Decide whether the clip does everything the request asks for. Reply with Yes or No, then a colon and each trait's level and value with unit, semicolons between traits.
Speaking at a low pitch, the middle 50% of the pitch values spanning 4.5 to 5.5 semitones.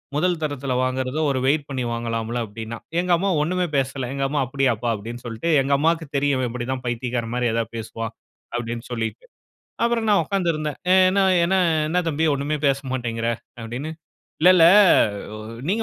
Yes: low, 130 Hz; average, 4.9 semitones